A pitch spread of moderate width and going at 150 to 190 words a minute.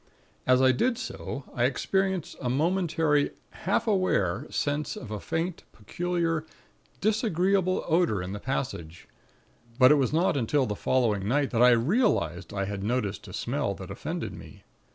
No: wide, 7.5 semitones; average, 155 wpm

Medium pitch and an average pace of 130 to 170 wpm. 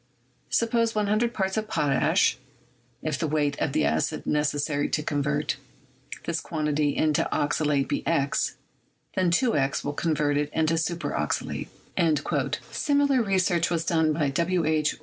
Yes: medium, 155 Hz; average, 140 wpm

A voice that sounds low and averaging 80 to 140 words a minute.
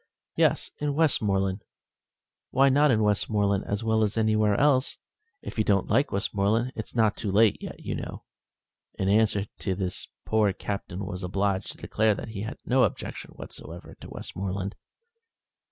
No: low, 105 Hz; average, 165 wpm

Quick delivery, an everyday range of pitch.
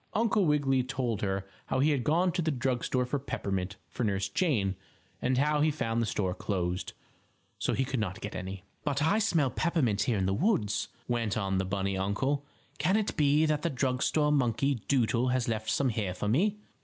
No: fast, 210 wpm; wide, 6.4 semitones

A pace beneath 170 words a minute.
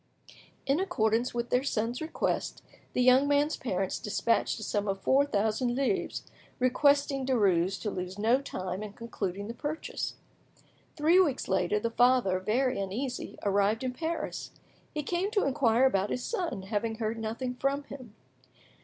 Yes: average, 155 wpm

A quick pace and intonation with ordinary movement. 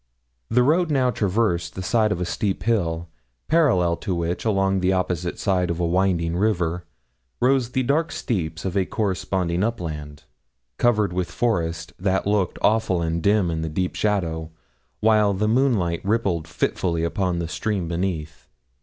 No: average, 160 wpm; average, 4.1 semitones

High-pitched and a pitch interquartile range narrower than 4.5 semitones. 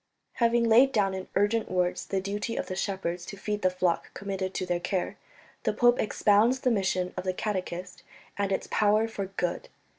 Yes: high, 195 Hz; average, 2.7 semitones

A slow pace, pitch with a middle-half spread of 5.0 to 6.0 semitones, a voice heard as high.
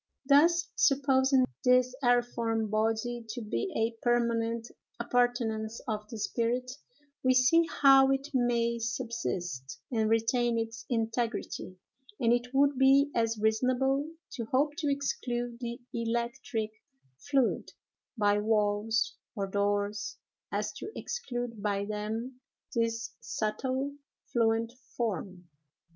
No: slow, 115 wpm; average, 2.7 semitones; high, 235 Hz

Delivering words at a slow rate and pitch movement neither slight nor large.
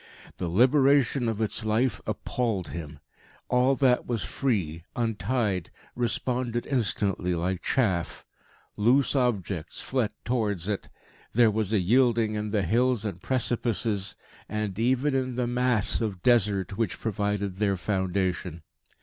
Yes: slow, 130 wpm; average, 4.1 semitones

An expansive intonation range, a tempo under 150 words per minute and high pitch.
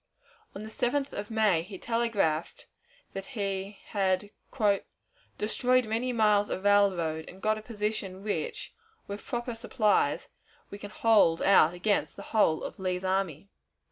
No: average, 2.7 semitones; average, 140 wpm; high, 205 Hz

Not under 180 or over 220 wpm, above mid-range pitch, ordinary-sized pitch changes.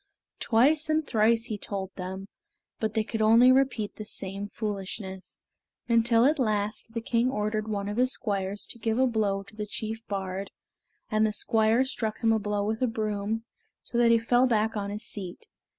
No: average, 190 wpm; high, 220 Hz; narrow, 2.2 semitones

